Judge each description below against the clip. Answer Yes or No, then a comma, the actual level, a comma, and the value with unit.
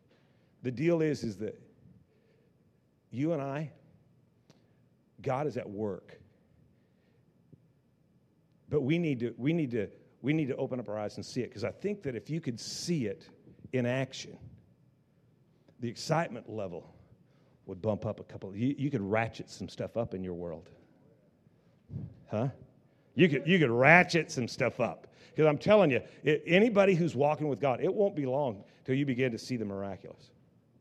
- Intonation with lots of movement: No, average, 4.7 semitones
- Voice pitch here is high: No, low, 135 Hz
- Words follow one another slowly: No, average, 170 wpm